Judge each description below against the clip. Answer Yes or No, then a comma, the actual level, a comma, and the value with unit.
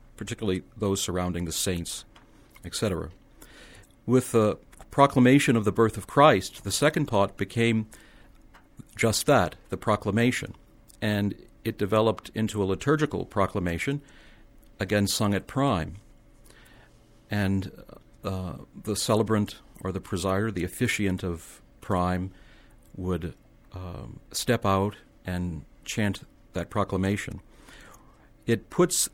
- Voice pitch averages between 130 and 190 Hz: No, low, 105 Hz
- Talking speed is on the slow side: Yes, slow, 105 wpm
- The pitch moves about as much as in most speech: Yes, average, 3.3 semitones